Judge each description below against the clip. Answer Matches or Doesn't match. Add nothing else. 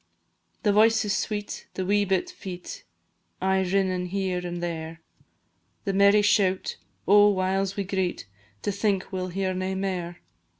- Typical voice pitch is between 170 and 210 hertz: Matches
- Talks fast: Doesn't match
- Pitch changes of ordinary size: Doesn't match